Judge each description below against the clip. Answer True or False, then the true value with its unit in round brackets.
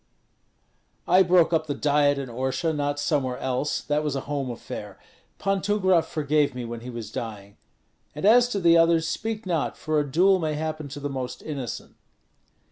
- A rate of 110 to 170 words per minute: False (185 wpm)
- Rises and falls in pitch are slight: False (4.1 semitones)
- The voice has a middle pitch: True (150 Hz)